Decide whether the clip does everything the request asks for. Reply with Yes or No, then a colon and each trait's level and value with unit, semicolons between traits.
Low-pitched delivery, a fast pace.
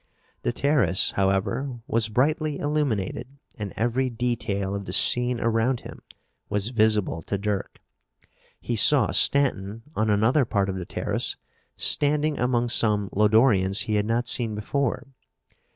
No: low, 115 Hz; slow, 135 wpm